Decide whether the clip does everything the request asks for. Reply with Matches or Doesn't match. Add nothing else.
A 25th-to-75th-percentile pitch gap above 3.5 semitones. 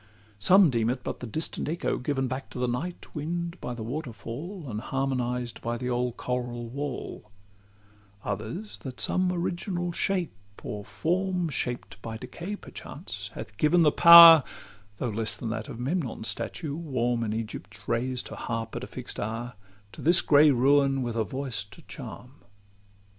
Matches